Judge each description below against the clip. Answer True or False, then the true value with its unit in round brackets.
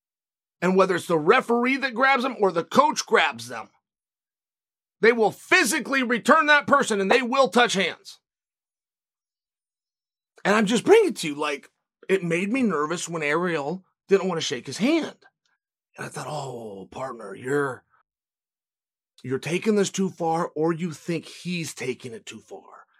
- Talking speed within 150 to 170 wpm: True (165 wpm)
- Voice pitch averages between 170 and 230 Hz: True (190 Hz)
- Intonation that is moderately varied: False (7.5 semitones)